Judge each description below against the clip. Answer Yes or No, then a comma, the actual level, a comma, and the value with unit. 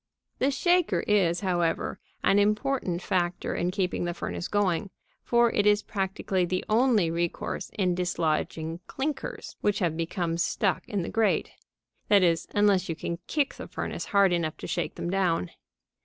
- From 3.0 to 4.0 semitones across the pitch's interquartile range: Yes, average, 3.3 semitones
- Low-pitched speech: No, medium, 185 Hz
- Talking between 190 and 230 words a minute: No, average, 160 wpm